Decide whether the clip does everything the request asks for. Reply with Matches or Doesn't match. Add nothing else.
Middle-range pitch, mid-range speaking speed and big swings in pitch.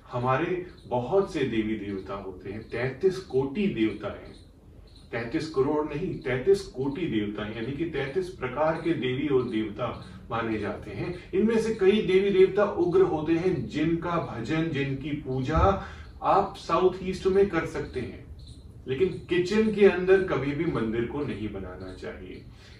Matches